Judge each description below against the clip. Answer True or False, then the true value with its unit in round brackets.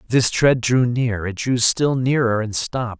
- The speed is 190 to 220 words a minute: True (200 wpm)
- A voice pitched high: False (120 Hz)